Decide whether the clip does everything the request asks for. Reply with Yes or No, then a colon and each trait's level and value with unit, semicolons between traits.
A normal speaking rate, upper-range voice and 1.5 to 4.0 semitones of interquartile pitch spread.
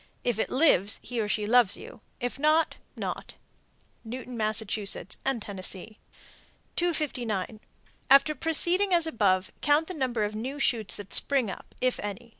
No: average, 150 wpm; high, 240 Hz; wide, 5.5 semitones